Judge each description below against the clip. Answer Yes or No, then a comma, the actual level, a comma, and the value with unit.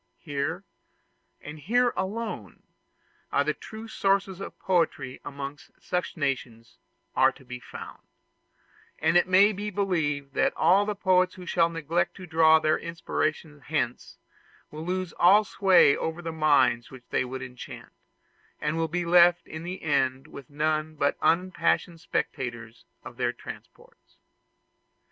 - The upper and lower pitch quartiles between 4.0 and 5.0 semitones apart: Yes, average, 4.4 semitones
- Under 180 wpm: Yes, average, 140 wpm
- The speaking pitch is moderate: Yes, medium, 160 Hz